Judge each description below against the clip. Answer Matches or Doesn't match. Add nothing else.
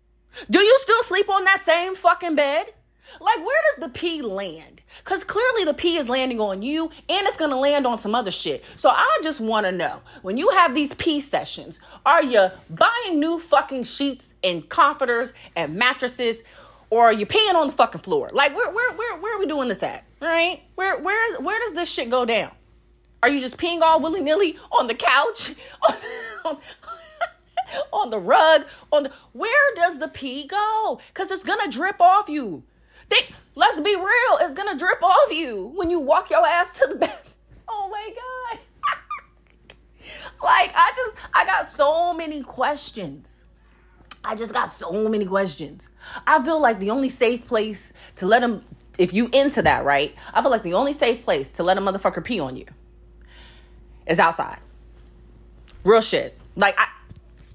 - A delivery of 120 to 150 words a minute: Doesn't match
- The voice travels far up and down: Matches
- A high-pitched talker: Matches